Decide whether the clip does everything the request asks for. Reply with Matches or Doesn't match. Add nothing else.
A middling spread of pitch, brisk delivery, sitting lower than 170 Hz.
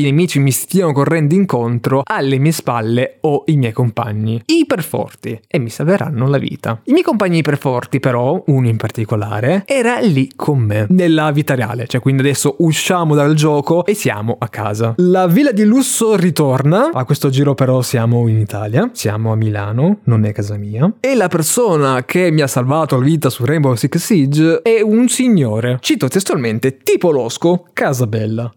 Doesn't match